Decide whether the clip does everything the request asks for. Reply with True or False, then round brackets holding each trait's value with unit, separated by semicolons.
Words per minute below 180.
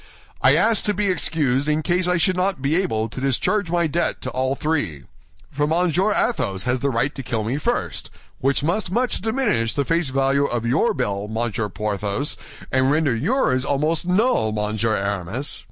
False (185 wpm)